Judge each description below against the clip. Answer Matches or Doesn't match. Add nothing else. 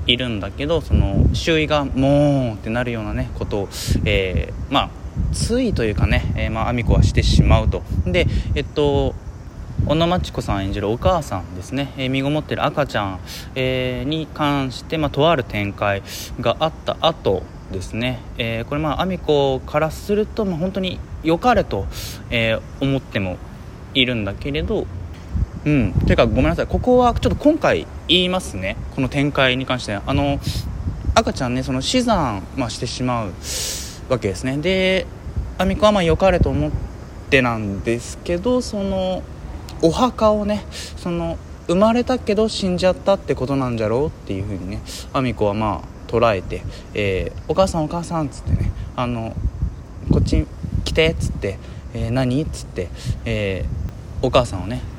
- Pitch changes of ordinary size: Doesn't match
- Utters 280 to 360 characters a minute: Matches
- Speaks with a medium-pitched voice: Doesn't match